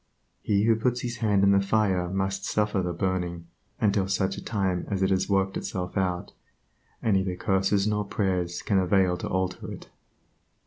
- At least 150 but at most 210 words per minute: Yes, average, 175 wpm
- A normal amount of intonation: No, narrow, 1.7 semitones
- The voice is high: No, very low, 95 Hz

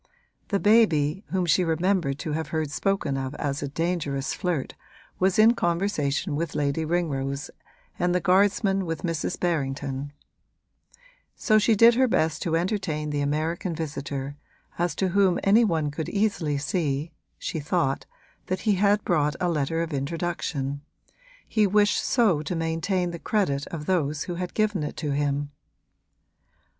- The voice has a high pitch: No, medium, 165 Hz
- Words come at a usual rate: Yes, average, 155 wpm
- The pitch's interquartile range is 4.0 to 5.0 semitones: Yes, average, 4.4 semitones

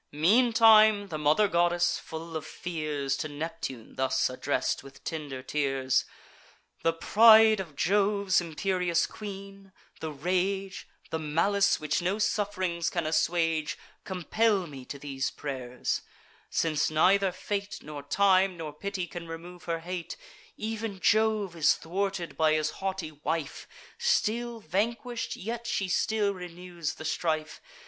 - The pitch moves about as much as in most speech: Yes, average, 4.4 semitones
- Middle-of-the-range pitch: Yes, medium, 175 Hz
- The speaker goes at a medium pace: No, slow, 130 wpm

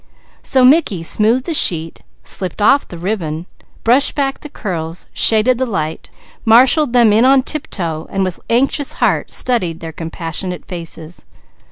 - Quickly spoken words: No, average, 150 wpm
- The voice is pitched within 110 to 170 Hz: No, high, 210 Hz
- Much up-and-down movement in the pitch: Yes, wide, 7.4 semitones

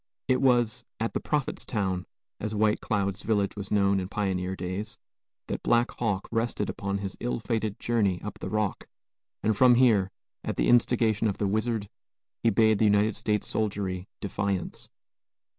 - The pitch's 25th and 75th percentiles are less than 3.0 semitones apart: Yes, narrow, 2.4 semitones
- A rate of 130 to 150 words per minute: No, average, 165 wpm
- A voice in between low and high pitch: No, low, 105 Hz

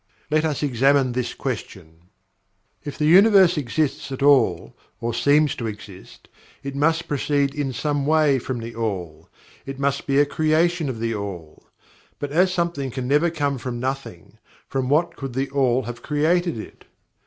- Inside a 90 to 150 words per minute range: No, average, 165 wpm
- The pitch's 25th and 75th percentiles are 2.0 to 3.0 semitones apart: No, average, 4.1 semitones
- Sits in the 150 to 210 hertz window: No, medium, 140 Hz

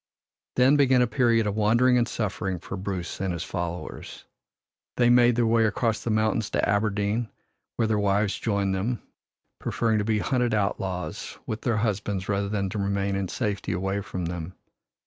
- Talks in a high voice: No, low, 105 Hz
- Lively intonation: No, average, 2.9 semitones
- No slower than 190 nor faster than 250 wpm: No, average, 175 wpm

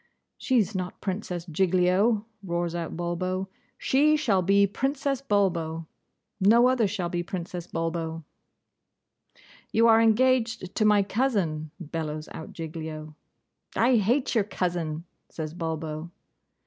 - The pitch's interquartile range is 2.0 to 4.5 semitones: No, average, 5.0 semitones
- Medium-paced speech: No, slow, 120 wpm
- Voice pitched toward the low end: No, medium, 185 Hz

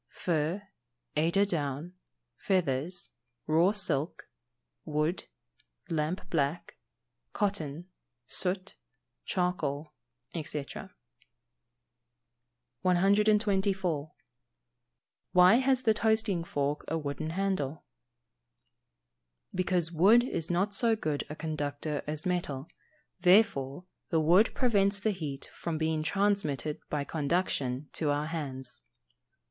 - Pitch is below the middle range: No, medium, 165 Hz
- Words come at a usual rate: No, slow, 95 wpm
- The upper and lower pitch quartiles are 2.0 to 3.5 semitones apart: No, average, 4.6 semitones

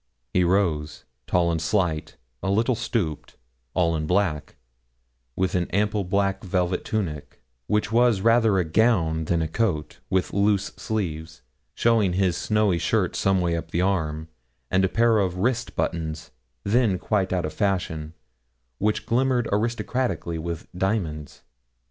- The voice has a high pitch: No, very low, 95 Hz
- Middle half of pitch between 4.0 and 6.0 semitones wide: Yes, average, 4.3 semitones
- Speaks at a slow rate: No, average, 145 wpm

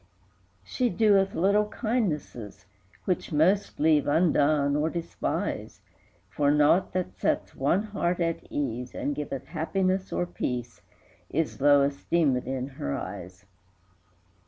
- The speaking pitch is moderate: Yes, medium, 155 Hz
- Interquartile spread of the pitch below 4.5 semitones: No, average, 4.8 semitones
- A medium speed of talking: No, slow, 125 wpm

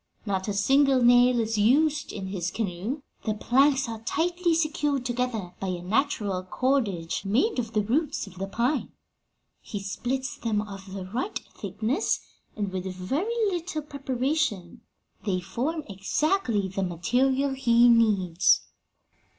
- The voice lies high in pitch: Yes, high, 235 Hz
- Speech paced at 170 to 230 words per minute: No, average, 140 wpm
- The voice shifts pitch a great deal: Yes, wide, 6.1 semitones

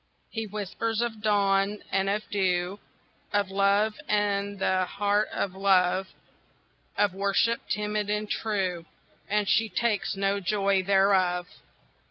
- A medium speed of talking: No, slow, 125 wpm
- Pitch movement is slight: Yes, narrow, 1.4 semitones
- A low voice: No, high, 200 Hz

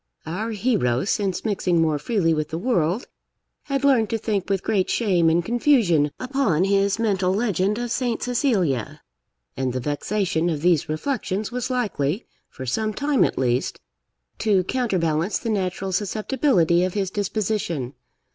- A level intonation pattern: No, wide, 5.5 semitones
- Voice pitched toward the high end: Yes, high, 195 Hz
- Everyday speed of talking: Yes, average, 150 wpm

